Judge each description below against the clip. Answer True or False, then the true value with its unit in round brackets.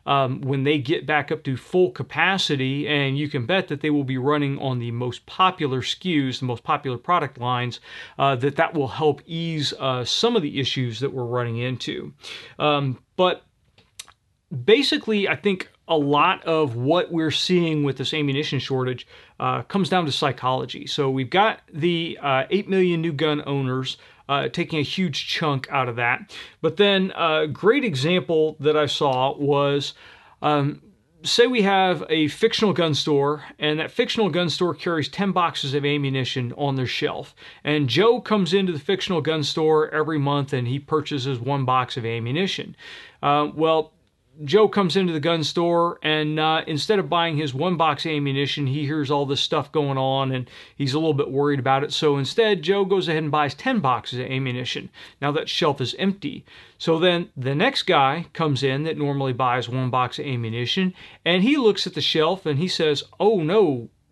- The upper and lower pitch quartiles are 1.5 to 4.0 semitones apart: True (3.7 semitones)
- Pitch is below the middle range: False (150 Hz)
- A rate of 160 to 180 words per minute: False (190 wpm)